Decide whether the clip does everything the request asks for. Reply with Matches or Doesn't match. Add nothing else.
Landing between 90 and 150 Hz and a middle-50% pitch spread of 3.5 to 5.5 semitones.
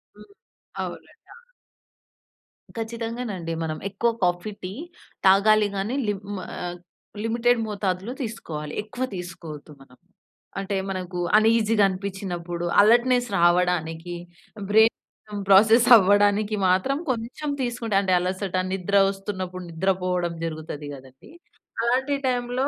Doesn't match